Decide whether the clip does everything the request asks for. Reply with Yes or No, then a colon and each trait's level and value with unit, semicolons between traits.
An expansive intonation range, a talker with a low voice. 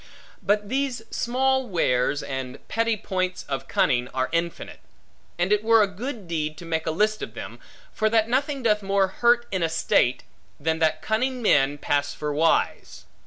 No: wide, 6.6 semitones; high, 190 Hz